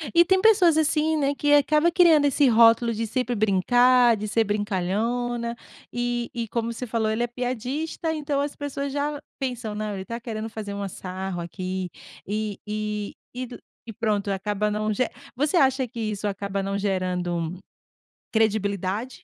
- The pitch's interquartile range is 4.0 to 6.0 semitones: Yes, average, 4.3 semitones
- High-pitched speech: Yes, high, 230 Hz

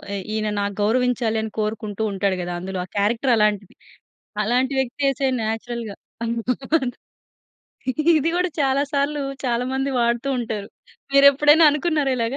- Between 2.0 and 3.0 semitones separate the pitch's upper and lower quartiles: No, average, 4.3 semitones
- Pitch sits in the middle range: No, high, 240 Hz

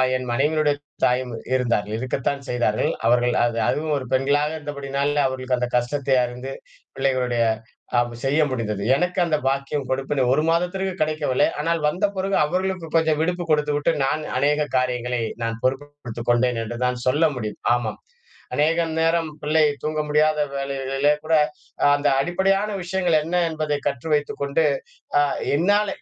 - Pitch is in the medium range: Yes, medium, 145 Hz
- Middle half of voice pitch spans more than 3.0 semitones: Yes, average, 3.9 semitones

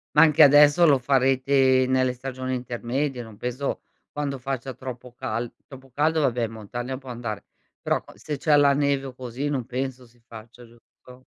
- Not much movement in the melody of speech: Yes, narrow, 2.3 semitones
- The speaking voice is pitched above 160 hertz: No, low, 130 Hz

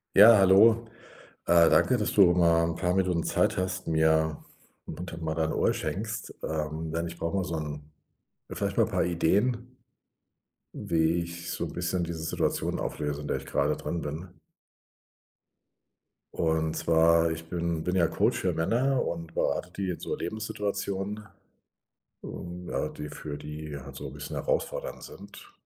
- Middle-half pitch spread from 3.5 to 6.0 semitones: No, average, 3.0 semitones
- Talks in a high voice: No, very low, 85 Hz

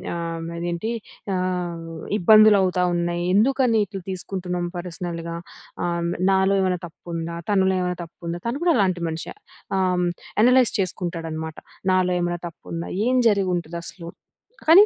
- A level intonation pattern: Yes, narrow, 2.2 semitones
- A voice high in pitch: No, medium, 180 Hz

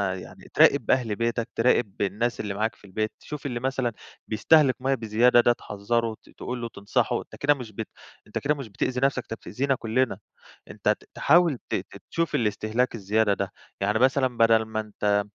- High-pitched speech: No, low, 115 Hz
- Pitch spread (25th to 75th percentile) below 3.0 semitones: No, average, 3.3 semitones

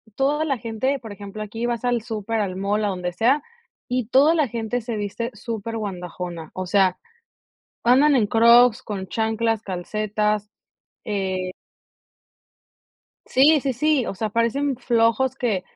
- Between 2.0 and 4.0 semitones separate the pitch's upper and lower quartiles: Yes, average, 3.5 semitones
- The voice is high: Yes, high, 225 Hz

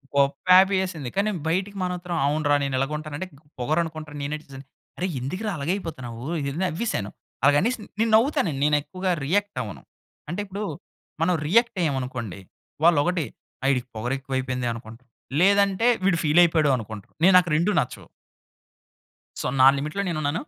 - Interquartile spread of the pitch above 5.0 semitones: Yes, wide, 5.4 semitones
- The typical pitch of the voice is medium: Yes, medium, 155 Hz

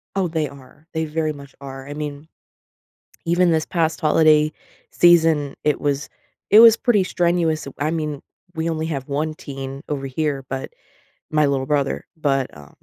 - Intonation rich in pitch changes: No, narrow, 2.5 semitones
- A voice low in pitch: No, medium, 150 Hz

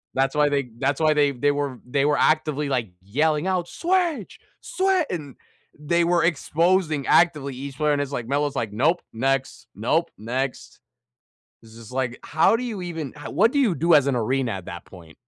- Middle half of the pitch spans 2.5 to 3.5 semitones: No, average, 4.3 semitones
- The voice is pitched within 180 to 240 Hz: No, medium, 145 Hz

